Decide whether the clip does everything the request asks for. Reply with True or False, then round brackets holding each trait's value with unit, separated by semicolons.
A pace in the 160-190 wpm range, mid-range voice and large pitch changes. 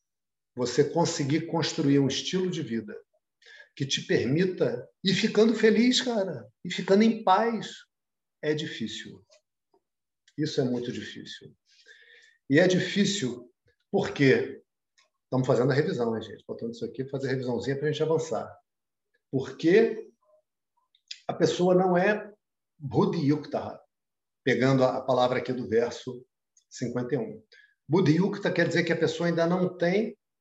False (130 wpm; 170 Hz; 7.9 semitones)